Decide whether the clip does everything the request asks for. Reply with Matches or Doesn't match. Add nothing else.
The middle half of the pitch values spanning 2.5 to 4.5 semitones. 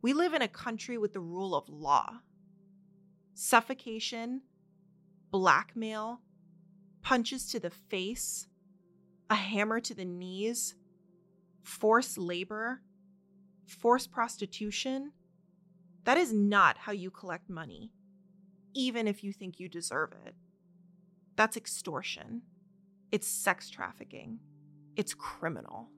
Matches